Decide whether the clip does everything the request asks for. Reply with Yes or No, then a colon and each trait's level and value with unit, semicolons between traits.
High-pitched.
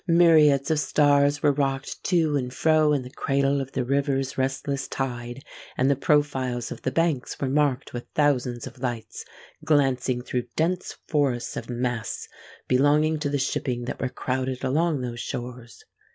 No: low, 135 Hz